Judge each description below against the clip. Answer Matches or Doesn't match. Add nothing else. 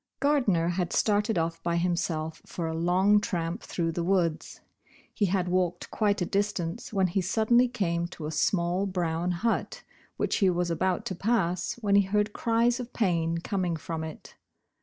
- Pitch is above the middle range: Doesn't match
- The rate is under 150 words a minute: Doesn't match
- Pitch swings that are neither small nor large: Matches